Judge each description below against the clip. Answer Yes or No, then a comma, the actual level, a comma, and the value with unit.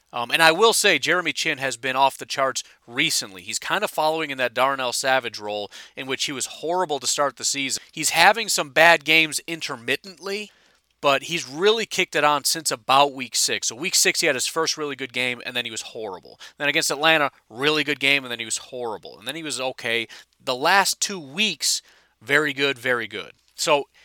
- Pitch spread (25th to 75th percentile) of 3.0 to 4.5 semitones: Yes, average, 4.1 semitones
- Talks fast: Yes, fast, 215 wpm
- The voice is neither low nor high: Yes, medium, 145 Hz